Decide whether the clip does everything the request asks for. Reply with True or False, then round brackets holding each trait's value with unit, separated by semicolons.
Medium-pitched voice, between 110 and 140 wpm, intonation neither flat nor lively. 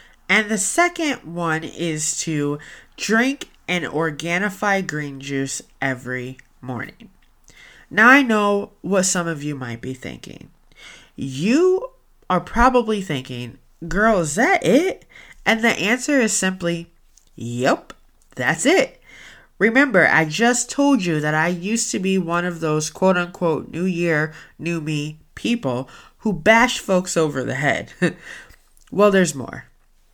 False (175 Hz; 135 wpm; 6.4 semitones)